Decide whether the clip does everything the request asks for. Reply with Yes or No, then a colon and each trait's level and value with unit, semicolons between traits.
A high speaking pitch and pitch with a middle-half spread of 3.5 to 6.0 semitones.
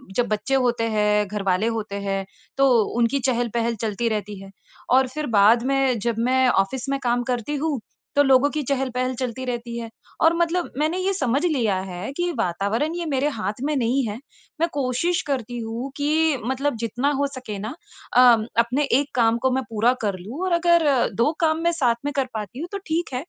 Yes: very high, 255 Hz; average, 4.2 semitones